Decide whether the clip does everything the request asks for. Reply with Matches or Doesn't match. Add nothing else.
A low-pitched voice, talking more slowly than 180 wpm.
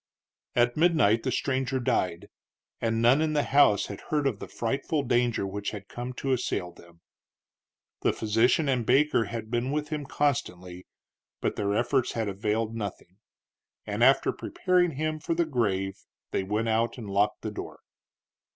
Matches